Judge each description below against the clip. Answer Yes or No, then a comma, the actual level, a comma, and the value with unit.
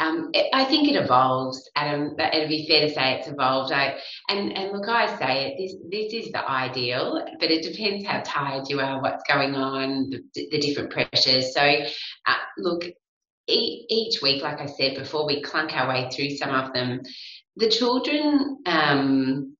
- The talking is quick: No, average, 190 wpm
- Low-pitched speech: No, medium, 145 Hz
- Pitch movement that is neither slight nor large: No, wide, 6.7 semitones